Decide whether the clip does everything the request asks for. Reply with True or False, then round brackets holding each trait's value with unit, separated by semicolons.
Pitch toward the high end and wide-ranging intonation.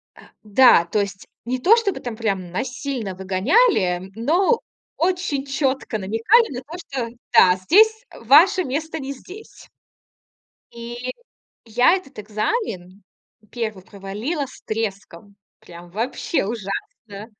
True (240 Hz; 7.8 semitones)